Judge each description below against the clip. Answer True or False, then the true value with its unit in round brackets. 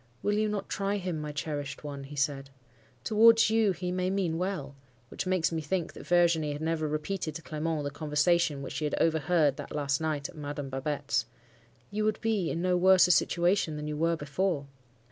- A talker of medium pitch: True (160 Hz)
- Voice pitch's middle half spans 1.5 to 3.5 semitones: False (4.0 semitones)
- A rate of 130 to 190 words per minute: False (200 wpm)